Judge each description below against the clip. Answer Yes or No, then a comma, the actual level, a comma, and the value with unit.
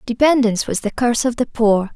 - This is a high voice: Yes, high, 235 Hz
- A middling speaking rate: No, fast, 215 wpm